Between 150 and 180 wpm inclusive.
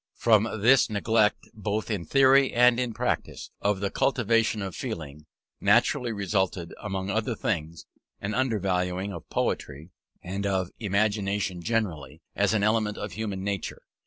No: average, 140 wpm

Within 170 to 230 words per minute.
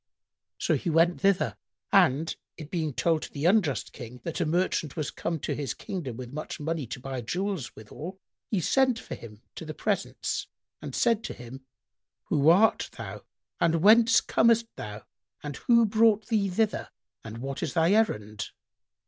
Yes: average, 175 wpm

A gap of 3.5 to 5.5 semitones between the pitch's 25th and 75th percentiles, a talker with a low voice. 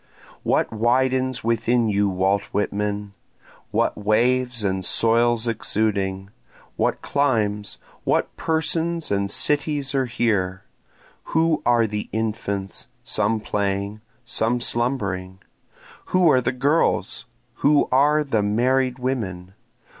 Yes: average, 4.2 semitones; low, 115 Hz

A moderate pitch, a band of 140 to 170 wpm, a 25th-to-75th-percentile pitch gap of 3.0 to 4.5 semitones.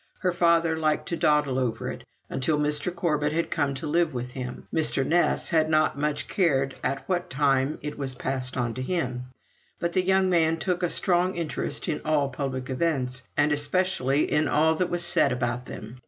No: medium, 150 Hz; average, 195 wpm; average, 4.2 semitones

